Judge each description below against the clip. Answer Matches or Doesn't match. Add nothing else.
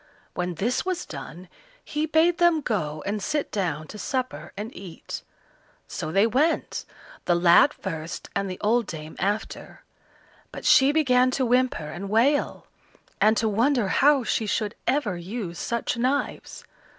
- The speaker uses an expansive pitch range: Matches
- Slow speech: Doesn't match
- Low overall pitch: Doesn't match